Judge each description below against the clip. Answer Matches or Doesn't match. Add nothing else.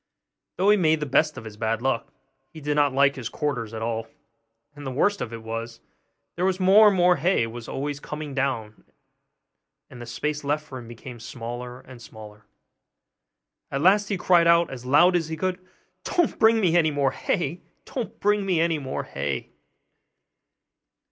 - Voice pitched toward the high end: Doesn't match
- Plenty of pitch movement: Matches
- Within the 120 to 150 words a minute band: Doesn't match